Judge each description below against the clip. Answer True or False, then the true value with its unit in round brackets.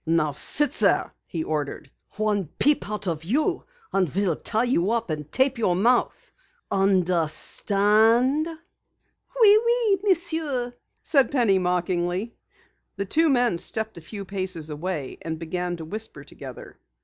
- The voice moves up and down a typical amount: False (6.9 semitones)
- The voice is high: True (200 Hz)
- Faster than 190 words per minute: False (135 wpm)